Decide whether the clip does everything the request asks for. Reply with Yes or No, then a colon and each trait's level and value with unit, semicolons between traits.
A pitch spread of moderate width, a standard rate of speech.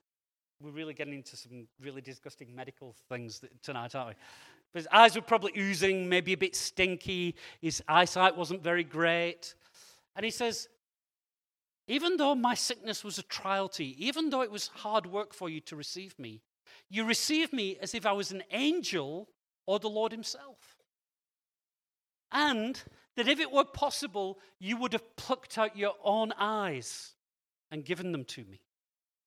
No: wide, 6.7 semitones; average, 170 wpm